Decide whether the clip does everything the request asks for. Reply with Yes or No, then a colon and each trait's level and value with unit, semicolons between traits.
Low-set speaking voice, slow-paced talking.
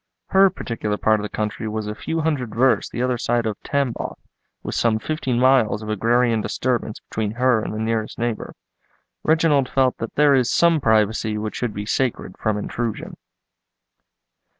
No: low, 115 Hz; average, 175 wpm